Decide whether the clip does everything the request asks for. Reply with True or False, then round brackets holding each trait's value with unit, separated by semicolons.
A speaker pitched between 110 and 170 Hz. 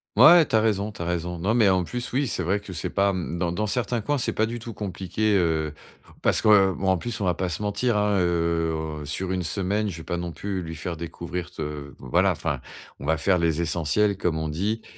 False (95 Hz)